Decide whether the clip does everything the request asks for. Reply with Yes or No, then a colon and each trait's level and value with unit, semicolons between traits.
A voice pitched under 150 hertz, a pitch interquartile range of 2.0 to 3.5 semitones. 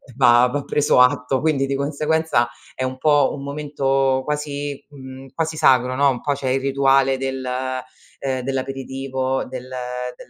No: low, 135 Hz; narrow, 1.5 semitones